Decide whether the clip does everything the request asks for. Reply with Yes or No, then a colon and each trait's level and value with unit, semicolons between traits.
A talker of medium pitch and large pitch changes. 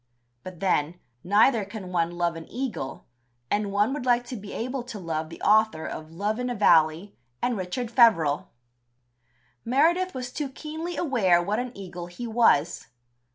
No: high, 210 Hz; wide, 6.1 semitones